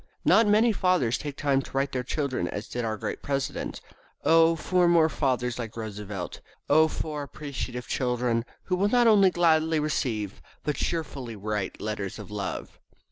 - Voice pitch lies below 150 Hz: Yes, medium, 140 Hz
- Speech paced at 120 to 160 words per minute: No, average, 170 wpm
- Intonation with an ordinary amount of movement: No, wide, 6.1 semitones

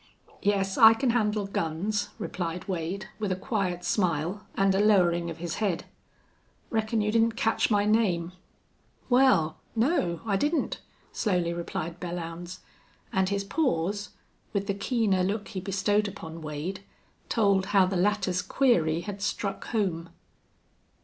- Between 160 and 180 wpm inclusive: No, average, 140 wpm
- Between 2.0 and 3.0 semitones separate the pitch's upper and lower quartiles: No, average, 3.4 semitones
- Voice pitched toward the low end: No, high, 195 Hz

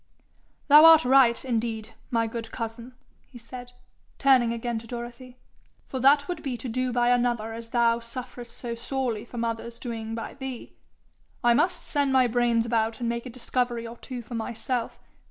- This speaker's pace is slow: No, average, 175 wpm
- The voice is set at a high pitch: Yes, high, 240 Hz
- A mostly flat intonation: Yes, narrow, 1.7 semitones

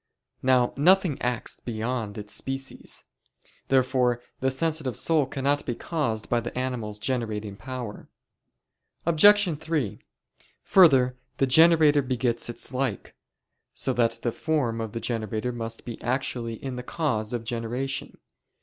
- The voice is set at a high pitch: No, low, 125 Hz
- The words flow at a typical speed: No, slow, 130 wpm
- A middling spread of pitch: Yes, average, 3.2 semitones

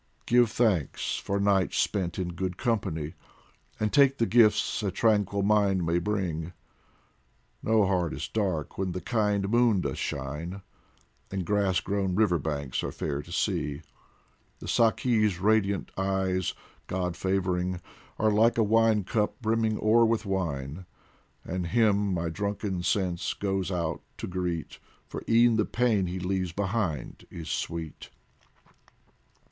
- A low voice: Yes, very low, 95 Hz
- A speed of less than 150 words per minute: Yes, average, 140 wpm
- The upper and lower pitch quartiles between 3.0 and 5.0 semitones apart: Yes, average, 3.5 semitones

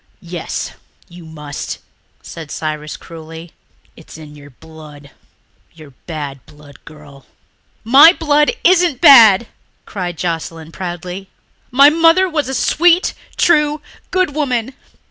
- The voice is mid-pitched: Yes, medium, 175 Hz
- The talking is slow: Yes, slow, 115 wpm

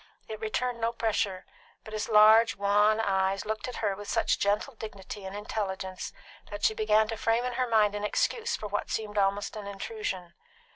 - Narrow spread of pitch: Yes, narrow, 1.9 semitones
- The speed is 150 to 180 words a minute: No, average, 190 wpm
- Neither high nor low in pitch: No, high, 210 Hz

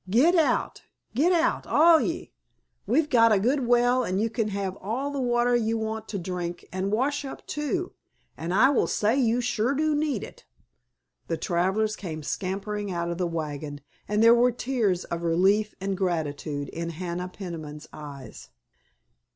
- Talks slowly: No, average, 175 wpm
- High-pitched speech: Yes, high, 210 Hz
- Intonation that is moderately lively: No, wide, 6.0 semitones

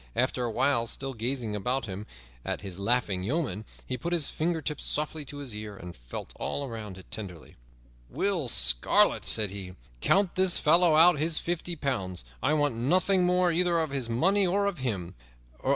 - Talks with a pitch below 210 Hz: Yes, low, 135 Hz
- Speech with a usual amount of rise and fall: No, wide, 7.9 semitones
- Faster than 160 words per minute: Yes, average, 180 wpm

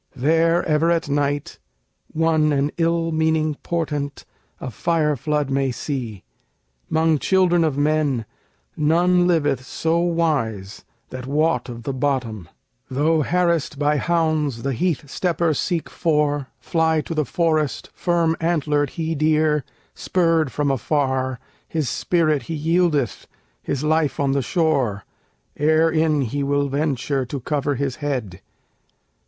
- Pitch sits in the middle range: Yes, medium, 150 Hz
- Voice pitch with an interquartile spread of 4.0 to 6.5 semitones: No, average, 3.0 semitones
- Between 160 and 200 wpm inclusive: No, slow, 135 wpm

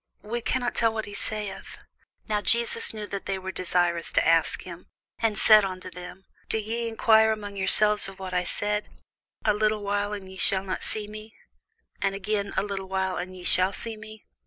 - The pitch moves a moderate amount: No, narrow, 2.3 semitones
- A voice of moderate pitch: No, high, 205 Hz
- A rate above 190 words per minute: Yes, average, 200 wpm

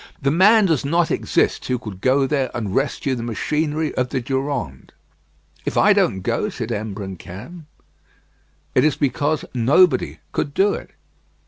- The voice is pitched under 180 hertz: Yes, low, 135 Hz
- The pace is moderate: Yes, average, 150 wpm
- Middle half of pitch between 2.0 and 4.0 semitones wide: No, average, 5.0 semitones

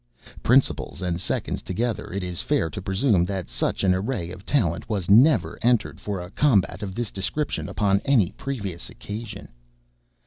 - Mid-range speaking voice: No, low, 100 Hz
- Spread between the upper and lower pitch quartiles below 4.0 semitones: No, average, 4.6 semitones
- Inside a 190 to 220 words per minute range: No, average, 165 wpm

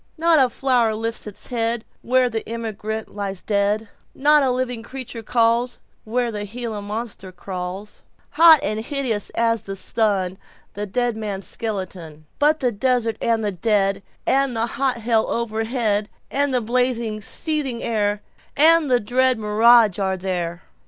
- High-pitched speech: Yes, high, 225 Hz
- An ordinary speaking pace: No, slow, 130 wpm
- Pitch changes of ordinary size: Yes, average, 3.4 semitones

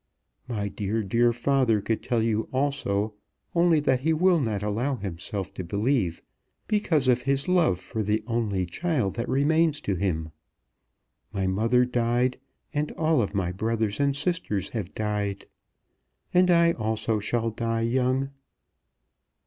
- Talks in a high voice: No, low, 115 Hz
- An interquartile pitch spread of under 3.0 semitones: No, average, 5.1 semitones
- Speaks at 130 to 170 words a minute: Yes, average, 140 wpm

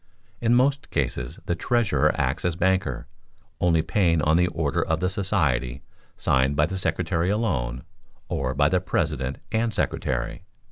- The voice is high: No, very low, 85 Hz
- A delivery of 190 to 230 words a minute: No, average, 150 wpm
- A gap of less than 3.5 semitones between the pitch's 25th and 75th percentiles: No, wide, 5.6 semitones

